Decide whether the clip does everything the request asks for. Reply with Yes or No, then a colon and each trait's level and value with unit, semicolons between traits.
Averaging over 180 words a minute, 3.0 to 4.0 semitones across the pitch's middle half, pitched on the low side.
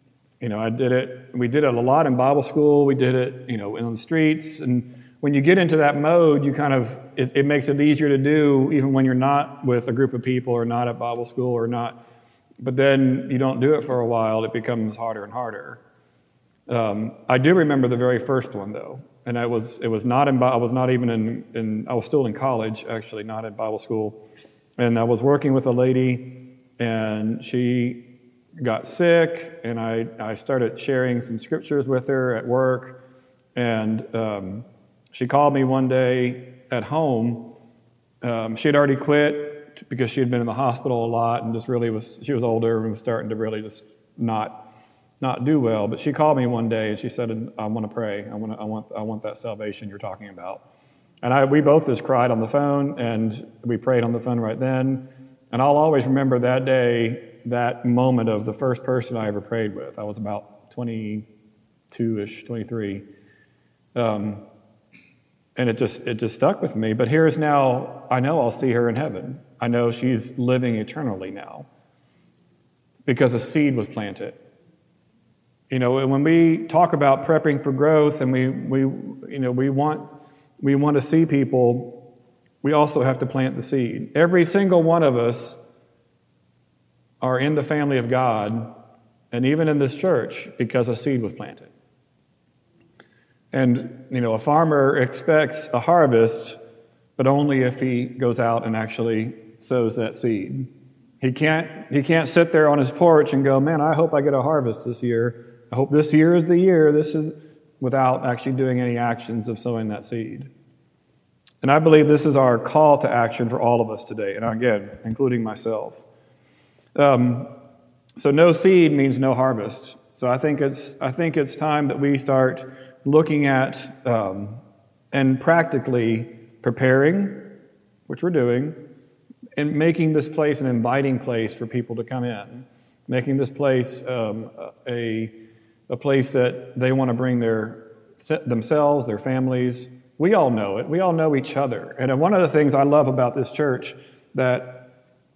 Yes: average, 190 wpm; average, 3.4 semitones; low, 125 Hz